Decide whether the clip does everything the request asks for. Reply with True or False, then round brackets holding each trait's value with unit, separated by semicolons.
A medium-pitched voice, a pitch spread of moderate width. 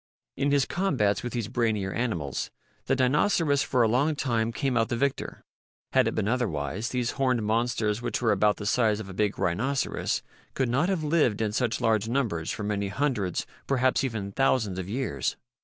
False (115 Hz; 4.1 semitones)